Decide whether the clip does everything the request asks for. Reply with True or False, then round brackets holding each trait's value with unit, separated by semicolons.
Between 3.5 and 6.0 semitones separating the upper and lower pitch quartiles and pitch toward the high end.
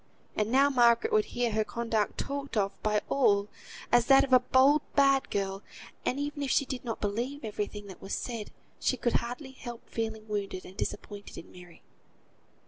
True (4.5 semitones; 235 Hz)